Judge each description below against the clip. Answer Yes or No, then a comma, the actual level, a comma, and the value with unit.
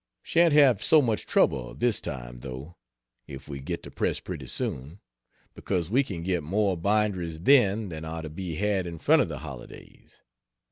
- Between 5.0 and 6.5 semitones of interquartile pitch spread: Yes, wide, 5.4 semitones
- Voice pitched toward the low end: Yes, very low, 90 Hz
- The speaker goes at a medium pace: Yes, average, 180 wpm